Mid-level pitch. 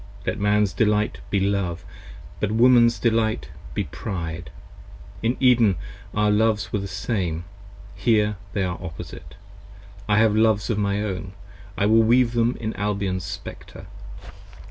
No: low, 105 Hz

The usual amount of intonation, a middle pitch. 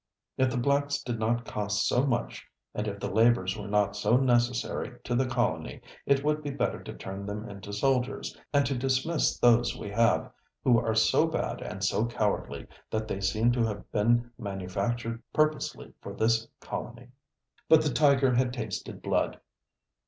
No: average, 3.8 semitones; low, 120 Hz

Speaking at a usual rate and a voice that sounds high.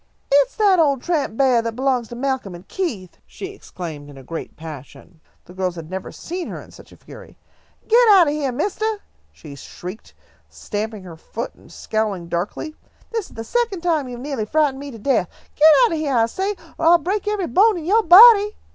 No: fast, 210 wpm; very high, 275 Hz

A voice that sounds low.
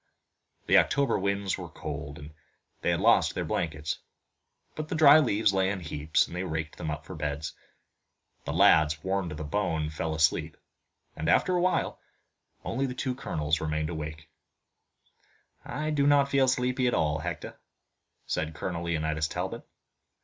Yes: very low, 85 Hz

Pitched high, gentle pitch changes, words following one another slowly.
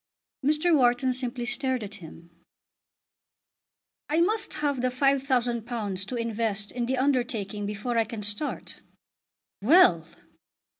No: high, 245 Hz; average, 4.1 semitones; slow, 115 wpm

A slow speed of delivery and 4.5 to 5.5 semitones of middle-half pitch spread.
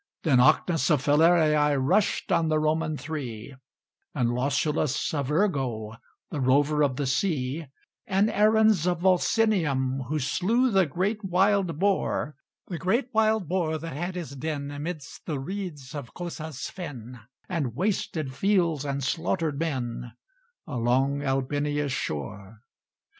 Yes: slow, 130 wpm; average, 5.0 semitones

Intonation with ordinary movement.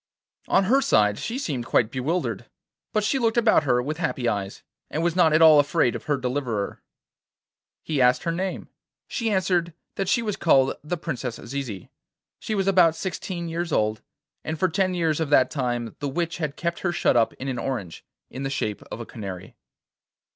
No: wide, 6.2 semitones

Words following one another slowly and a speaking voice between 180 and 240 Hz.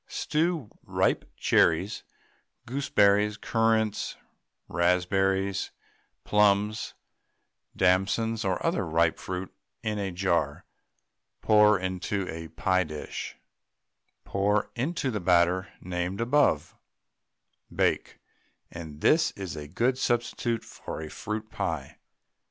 No: slow, 100 wpm; low, 100 Hz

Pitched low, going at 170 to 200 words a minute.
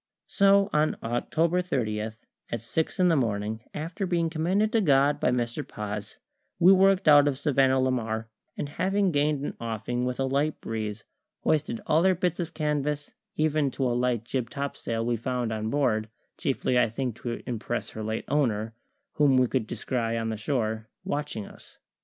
Yes: low, 130 Hz; average, 180 wpm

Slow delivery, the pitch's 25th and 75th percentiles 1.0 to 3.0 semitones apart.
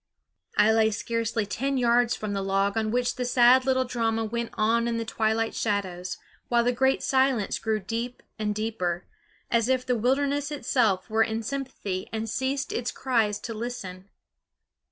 No: average, 170 wpm; narrow, 2.6 semitones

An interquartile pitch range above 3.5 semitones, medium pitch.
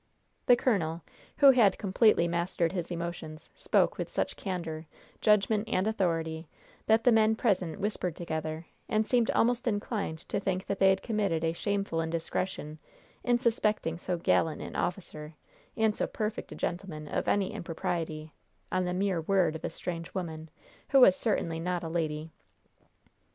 Yes: average, 4.5 semitones; medium, 180 Hz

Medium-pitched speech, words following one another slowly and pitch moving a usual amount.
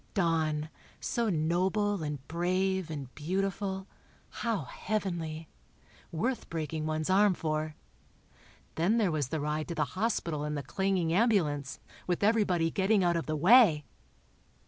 Yes: medium, 170 Hz; slow, 125 wpm; average, 4.0 semitones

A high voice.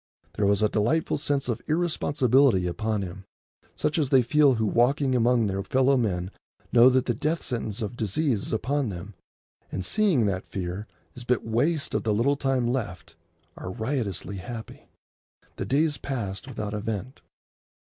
No: low, 120 Hz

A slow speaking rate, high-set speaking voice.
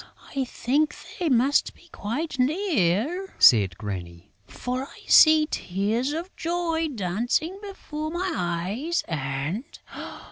Yes: slow, 115 wpm; very high, 265 Hz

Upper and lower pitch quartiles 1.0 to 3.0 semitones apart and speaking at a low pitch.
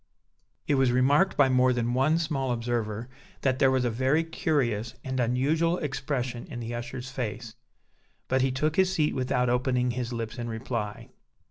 Yes: narrow, 2.4 semitones; low, 130 Hz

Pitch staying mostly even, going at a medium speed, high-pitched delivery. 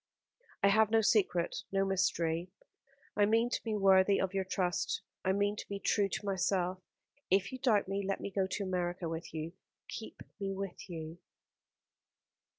Yes: narrow, 2.0 semitones; average, 170 wpm; high, 195 Hz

